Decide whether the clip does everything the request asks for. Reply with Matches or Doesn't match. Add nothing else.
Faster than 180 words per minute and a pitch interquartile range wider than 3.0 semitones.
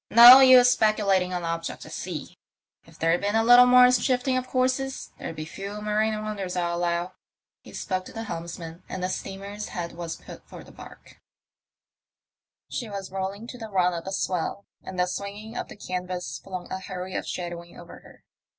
Matches